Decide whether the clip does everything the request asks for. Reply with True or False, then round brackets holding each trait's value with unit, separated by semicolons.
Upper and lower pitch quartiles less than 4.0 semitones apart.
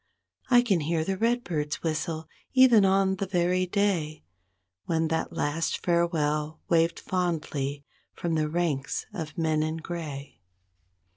True (3.1 semitones)